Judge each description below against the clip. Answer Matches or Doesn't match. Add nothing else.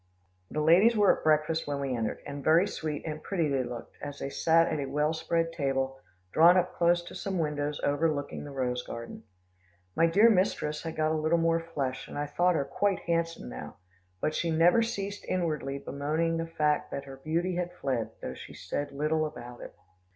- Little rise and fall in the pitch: Doesn't match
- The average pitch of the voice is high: Doesn't match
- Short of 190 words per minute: Doesn't match